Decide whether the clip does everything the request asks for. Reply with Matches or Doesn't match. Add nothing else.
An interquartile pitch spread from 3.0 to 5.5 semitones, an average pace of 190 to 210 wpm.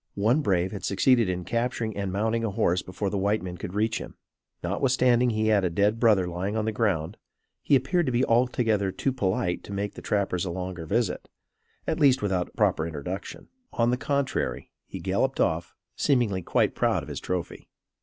Matches